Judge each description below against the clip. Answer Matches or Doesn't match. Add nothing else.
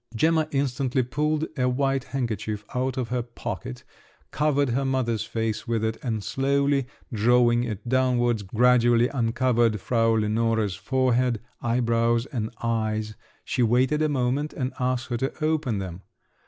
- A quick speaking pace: Doesn't match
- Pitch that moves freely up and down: Doesn't match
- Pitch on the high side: Doesn't match